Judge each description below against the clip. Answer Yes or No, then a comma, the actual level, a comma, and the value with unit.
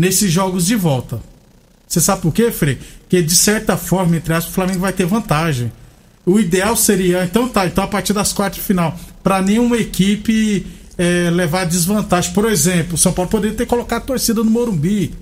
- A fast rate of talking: Yes, fast, 195 wpm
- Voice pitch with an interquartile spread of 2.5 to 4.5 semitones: Yes, average, 3.3 semitones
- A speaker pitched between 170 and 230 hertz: Yes, high, 190 Hz